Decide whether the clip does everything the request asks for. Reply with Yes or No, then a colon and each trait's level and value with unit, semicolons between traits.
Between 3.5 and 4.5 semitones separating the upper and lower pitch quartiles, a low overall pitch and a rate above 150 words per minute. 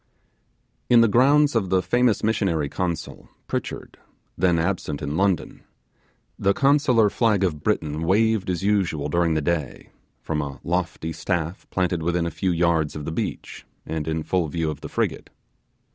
Yes: average, 4.2 semitones; very low, 90 Hz; average, 160 wpm